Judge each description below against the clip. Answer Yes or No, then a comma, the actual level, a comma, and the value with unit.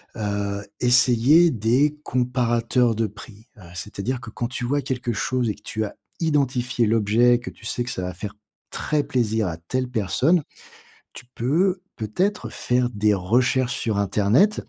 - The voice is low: Yes, low, 120 Hz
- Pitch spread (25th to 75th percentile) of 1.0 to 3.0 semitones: No, average, 3.4 semitones